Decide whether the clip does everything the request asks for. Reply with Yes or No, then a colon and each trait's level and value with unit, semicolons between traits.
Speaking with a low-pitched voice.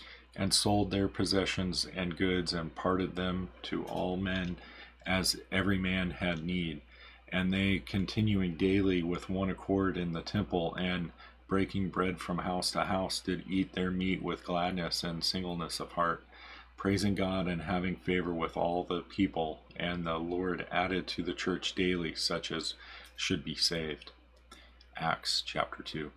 Yes: very low, 90 Hz